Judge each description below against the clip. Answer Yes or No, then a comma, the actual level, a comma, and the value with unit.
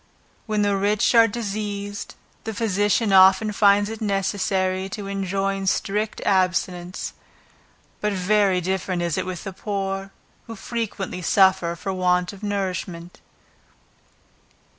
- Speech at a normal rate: No, slow, 120 wpm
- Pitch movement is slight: Yes, narrow, 1.8 semitones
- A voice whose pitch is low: No, high, 195 Hz